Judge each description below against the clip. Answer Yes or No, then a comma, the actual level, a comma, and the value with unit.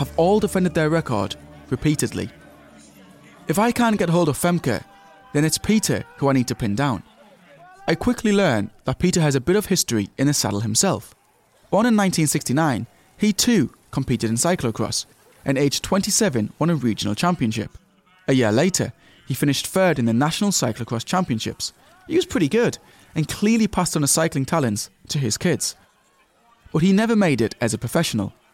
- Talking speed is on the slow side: No, average, 175 wpm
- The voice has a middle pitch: Yes, medium, 145 Hz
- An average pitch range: No, wide, 8.1 semitones